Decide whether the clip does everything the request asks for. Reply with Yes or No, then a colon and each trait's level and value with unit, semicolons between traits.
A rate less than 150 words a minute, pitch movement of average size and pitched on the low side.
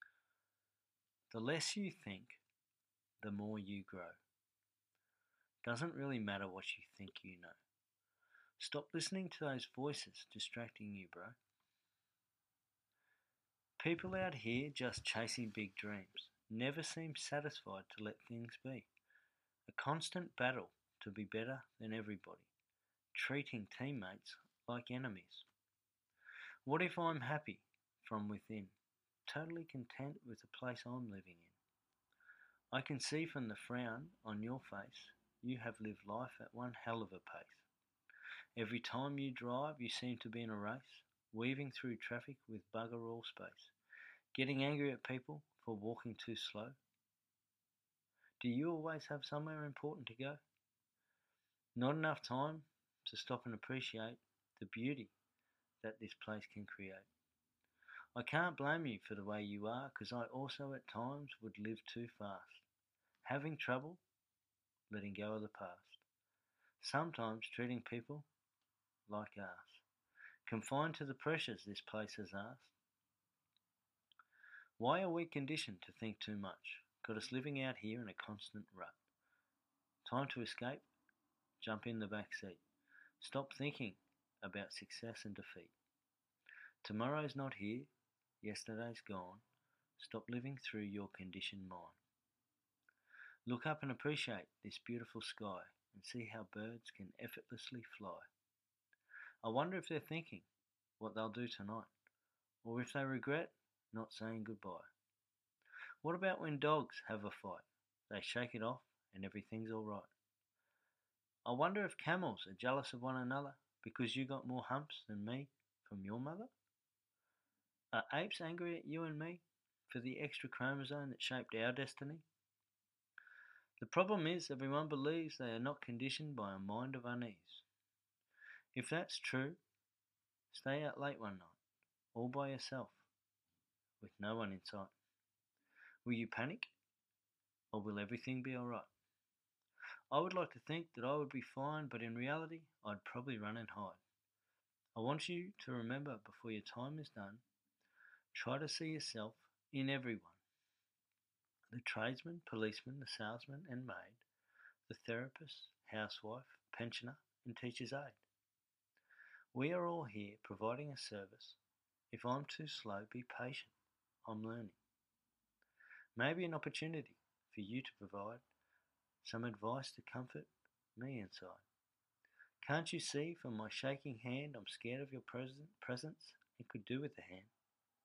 Yes: average, 140 wpm; average, 4.7 semitones; low, 120 Hz